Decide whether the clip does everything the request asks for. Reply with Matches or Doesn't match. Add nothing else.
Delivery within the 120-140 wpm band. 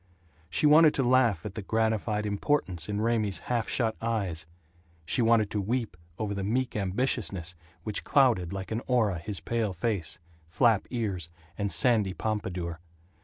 Doesn't match